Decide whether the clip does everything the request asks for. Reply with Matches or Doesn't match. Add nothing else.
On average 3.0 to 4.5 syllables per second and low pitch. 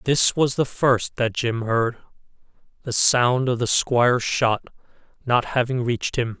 Matches